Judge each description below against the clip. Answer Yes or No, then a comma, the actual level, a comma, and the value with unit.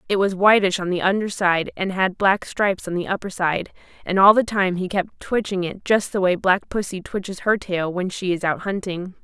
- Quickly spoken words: Yes, fast, 235 wpm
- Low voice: No, high, 190 Hz